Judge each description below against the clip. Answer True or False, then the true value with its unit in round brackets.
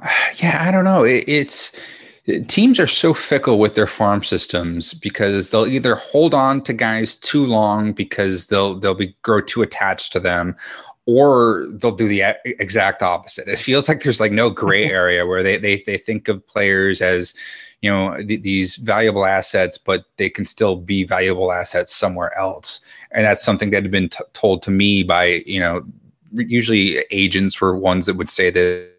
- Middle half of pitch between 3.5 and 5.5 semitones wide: False (2.7 semitones)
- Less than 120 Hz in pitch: True (100 Hz)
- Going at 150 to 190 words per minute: True (185 wpm)